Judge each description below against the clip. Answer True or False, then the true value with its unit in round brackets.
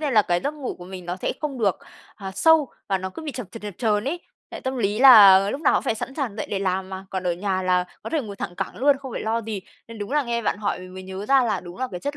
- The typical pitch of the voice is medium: False (210 Hz)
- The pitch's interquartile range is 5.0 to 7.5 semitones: True (5.6 semitones)